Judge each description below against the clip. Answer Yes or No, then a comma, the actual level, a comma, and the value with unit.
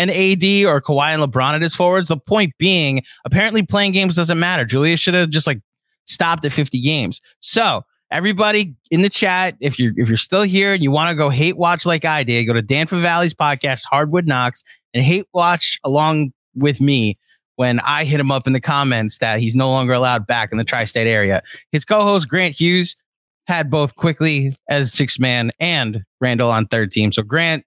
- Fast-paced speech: Yes, fast, 210 wpm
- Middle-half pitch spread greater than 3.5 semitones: Yes, wide, 5.6 semitones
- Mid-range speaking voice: Yes, medium, 150 Hz